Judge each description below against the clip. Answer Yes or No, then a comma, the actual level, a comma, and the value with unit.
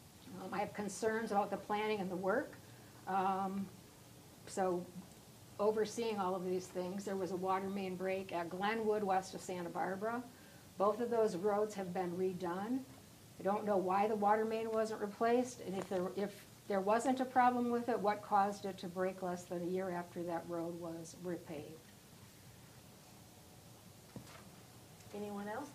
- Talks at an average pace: Yes, average, 165 wpm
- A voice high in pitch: Yes, high, 195 Hz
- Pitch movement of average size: No, narrow, 2.3 semitones